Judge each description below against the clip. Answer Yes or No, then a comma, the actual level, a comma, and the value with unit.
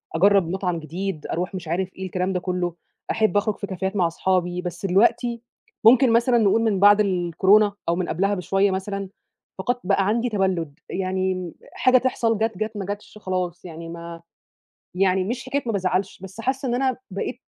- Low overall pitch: No, high, 190 Hz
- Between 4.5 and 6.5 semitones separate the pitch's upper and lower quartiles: No, average, 3.0 semitones